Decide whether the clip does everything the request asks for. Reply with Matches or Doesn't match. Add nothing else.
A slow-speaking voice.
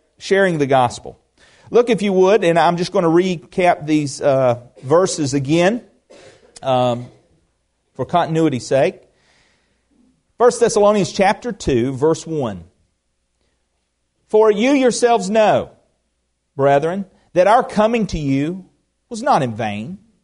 Matches